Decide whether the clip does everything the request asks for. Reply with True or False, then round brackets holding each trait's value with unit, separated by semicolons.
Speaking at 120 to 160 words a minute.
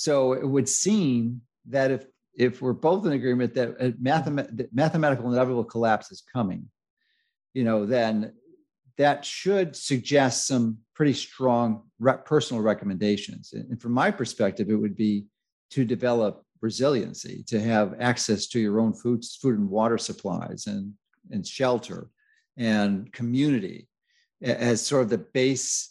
True (145 wpm)